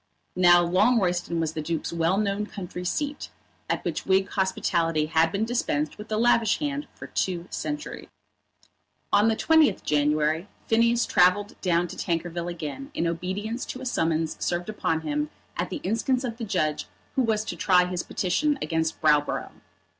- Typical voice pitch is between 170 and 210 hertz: Yes, medium, 185 Hz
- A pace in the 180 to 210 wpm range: No, average, 165 wpm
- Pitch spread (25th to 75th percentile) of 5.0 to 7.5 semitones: Yes, wide, 5.4 semitones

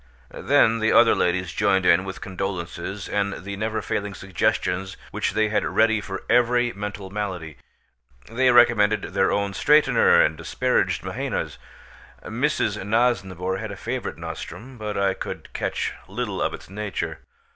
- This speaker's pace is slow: No, average, 145 wpm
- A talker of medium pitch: No, low, 100 Hz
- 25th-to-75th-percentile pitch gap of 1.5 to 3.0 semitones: Yes, average, 2.7 semitones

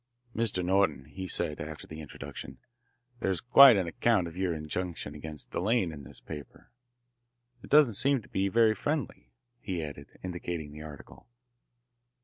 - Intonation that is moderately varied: No, wide, 5.7 semitones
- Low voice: Yes, very low, 90 Hz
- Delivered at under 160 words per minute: Yes, average, 150 wpm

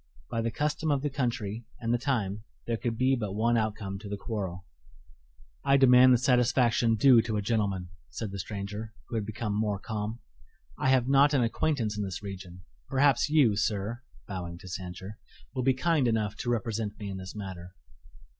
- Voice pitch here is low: Yes, low, 110 Hz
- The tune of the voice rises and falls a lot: No, average, 3.8 semitones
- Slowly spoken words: No, average, 190 wpm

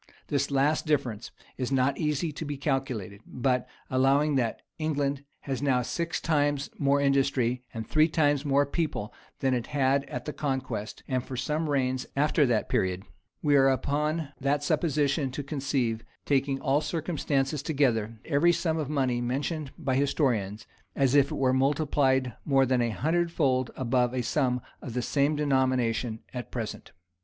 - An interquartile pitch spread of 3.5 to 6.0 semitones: No, narrow, 2.5 semitones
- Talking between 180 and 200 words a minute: No, average, 165 wpm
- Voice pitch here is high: No, low, 135 Hz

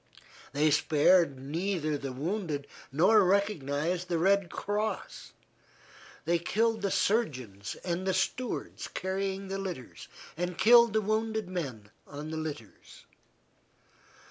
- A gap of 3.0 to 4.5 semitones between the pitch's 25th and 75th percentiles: No, average, 5.2 semitones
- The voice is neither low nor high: Yes, medium, 180 Hz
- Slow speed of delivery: Yes, slow, 115 wpm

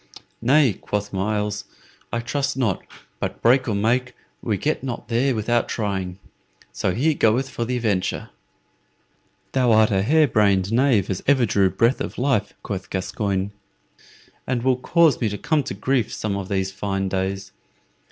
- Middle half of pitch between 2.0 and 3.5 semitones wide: No, average, 4.5 semitones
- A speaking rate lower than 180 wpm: Yes, average, 160 wpm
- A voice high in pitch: No, low, 110 Hz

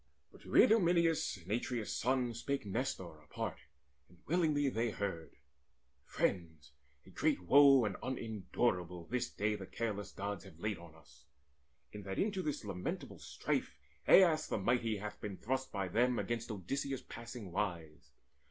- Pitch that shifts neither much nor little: No, wide, 5.7 semitones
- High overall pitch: No, low, 110 Hz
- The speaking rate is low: No, average, 150 wpm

